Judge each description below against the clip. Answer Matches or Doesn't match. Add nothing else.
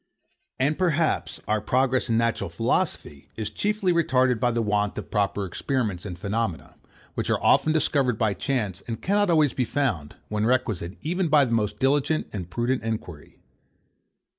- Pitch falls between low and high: Doesn't match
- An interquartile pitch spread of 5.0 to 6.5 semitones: Matches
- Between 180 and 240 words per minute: Doesn't match